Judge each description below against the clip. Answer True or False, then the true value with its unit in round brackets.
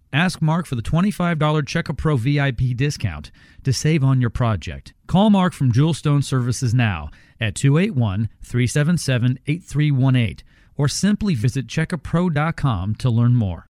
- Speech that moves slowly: True (125 wpm)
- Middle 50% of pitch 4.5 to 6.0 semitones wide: True (4.9 semitones)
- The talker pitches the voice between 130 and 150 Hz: True (135 Hz)